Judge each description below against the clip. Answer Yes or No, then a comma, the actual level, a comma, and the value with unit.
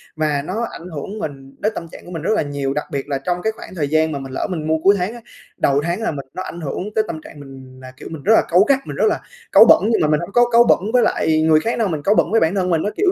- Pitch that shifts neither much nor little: No, wide, 5.7 semitones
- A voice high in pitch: No, medium, 160 Hz